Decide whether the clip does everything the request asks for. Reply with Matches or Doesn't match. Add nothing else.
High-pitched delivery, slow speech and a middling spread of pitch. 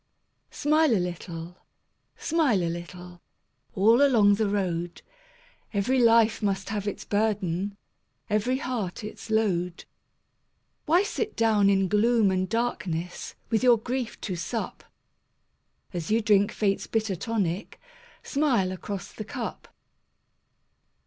Matches